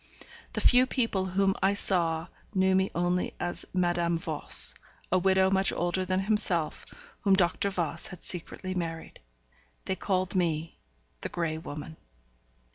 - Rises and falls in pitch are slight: Yes, narrow, 2.1 semitones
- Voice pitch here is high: No, medium, 180 Hz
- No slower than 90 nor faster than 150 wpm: Yes, average, 140 wpm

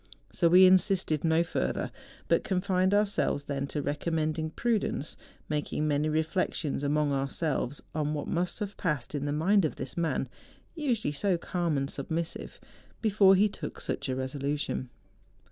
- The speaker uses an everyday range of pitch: Yes, average, 4.3 semitones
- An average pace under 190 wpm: Yes, average, 160 wpm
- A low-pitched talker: No, medium, 160 Hz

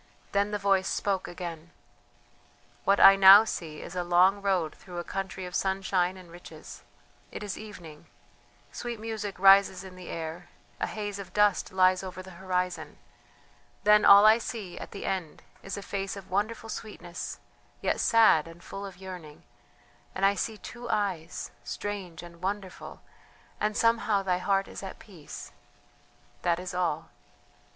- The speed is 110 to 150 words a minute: No, average, 160 wpm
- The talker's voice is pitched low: No, high, 190 Hz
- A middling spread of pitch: No, narrow, 2.2 semitones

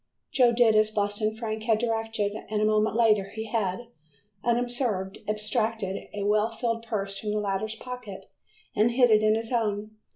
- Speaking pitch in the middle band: No, high, 215 Hz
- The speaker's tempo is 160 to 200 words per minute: Yes, average, 170 wpm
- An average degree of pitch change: No, narrow, 1.6 semitones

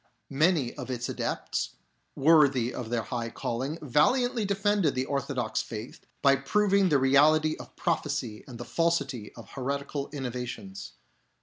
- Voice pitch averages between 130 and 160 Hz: Yes, medium, 140 Hz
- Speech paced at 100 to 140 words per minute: Yes, slow, 135 wpm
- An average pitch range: Yes, average, 4.2 semitones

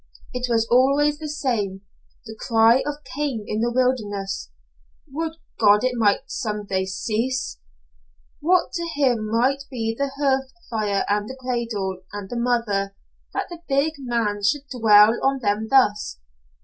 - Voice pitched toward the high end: Yes, high, 235 Hz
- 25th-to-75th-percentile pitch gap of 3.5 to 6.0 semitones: Yes, average, 4.3 semitones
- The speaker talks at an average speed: Yes, average, 150 wpm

